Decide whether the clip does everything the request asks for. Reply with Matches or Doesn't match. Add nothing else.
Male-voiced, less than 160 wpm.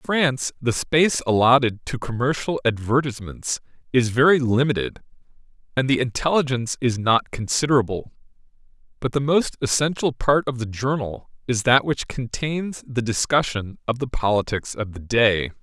Matches